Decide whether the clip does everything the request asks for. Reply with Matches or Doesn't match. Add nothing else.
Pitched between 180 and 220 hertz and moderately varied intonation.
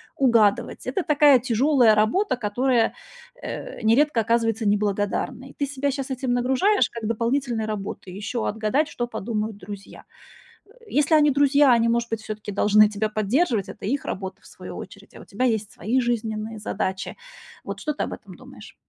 Doesn't match